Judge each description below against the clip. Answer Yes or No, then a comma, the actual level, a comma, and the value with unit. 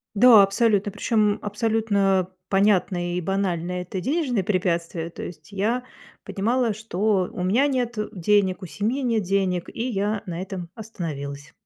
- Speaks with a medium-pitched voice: No, high, 200 Hz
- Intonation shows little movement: No, average, 3.6 semitones